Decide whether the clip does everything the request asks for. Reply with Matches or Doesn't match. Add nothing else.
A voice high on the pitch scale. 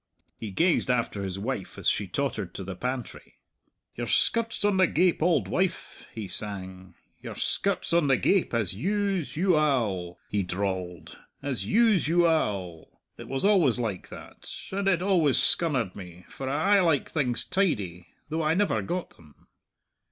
Doesn't match